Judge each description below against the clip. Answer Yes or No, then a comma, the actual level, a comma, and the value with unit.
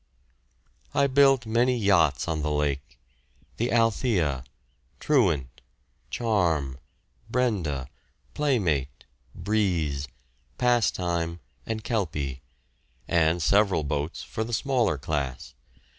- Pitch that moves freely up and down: Yes, wide, 7.7 semitones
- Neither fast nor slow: No, slow, 90 wpm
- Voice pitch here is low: Yes, very low, 85 Hz